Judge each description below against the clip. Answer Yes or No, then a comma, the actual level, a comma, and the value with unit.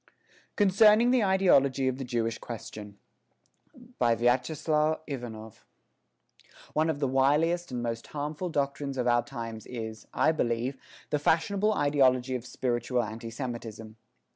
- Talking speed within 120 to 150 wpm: Yes, average, 140 wpm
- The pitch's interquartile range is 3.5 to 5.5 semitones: Yes, average, 4.6 semitones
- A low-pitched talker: Yes, low, 130 Hz